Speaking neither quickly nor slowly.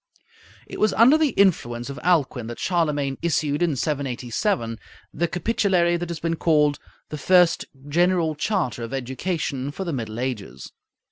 Yes: average, 150 wpm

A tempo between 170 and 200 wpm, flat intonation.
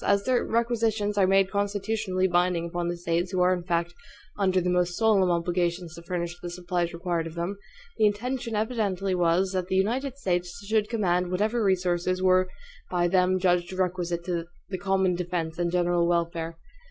Yes: average, 175 wpm; narrow, 2.3 semitones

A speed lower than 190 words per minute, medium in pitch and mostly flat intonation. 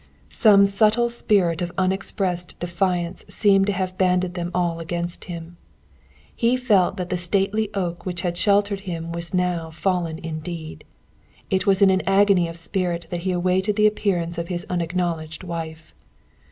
Yes: average, 160 wpm; medium, 180 Hz; narrow, 2.3 semitones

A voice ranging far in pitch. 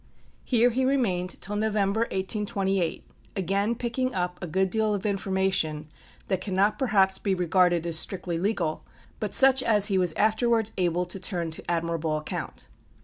No: average, 3.4 semitones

